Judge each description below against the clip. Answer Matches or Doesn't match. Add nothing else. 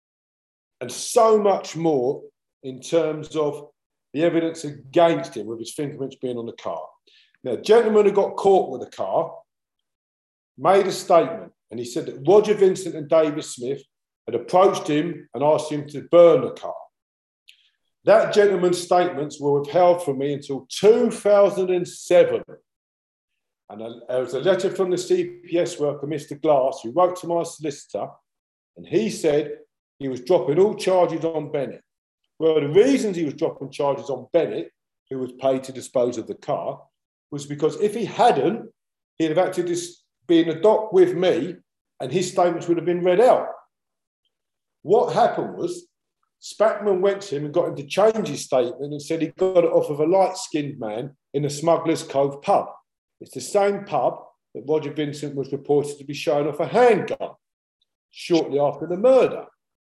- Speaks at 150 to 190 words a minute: Matches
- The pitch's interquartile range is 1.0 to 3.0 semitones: Doesn't match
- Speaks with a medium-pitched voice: Matches